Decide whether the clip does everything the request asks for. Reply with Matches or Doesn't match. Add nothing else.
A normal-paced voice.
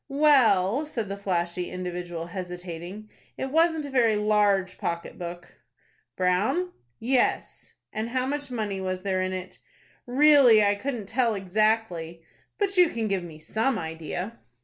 Matches